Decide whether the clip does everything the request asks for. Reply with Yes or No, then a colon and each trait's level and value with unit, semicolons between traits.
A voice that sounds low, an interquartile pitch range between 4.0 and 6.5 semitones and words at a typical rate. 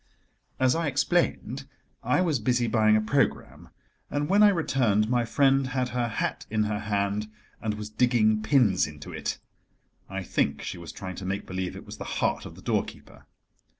Yes: low, 110 Hz; average, 4.3 semitones; average, 185 wpm